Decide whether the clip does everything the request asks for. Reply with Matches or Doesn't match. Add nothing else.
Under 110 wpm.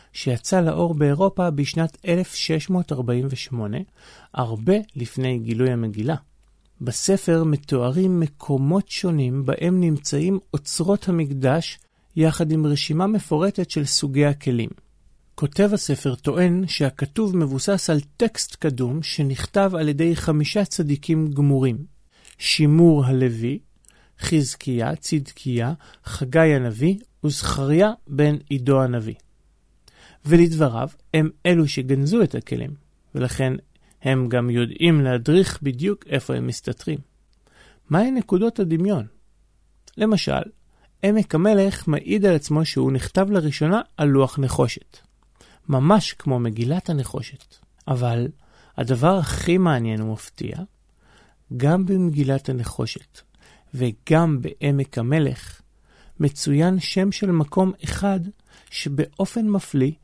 Matches